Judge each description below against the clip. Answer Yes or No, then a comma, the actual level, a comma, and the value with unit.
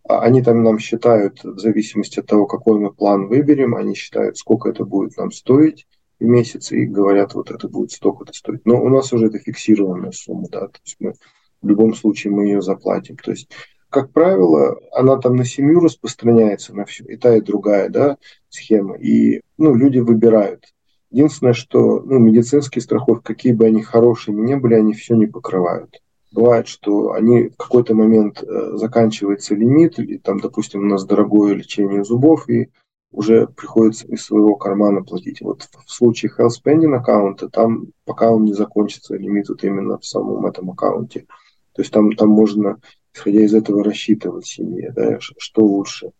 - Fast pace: Yes, fast, 175 wpm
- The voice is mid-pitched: No, low, 110 Hz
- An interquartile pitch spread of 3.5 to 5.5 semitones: No, narrow, 2.5 semitones